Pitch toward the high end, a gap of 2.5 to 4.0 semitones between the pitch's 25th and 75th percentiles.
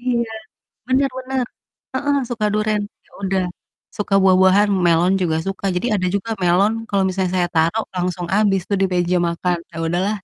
Yes: high, 195 Hz; average, 3.3 semitones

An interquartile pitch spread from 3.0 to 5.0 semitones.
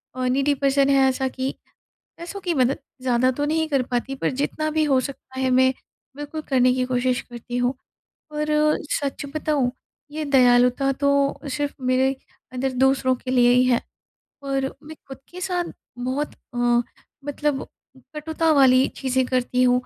No: narrow, 2.4 semitones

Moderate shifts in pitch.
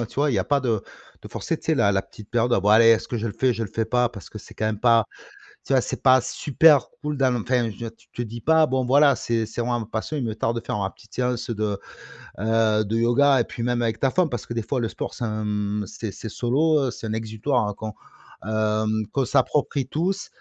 Yes: average, 3.1 semitones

